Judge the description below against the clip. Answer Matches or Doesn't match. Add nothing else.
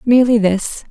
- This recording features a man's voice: Doesn't match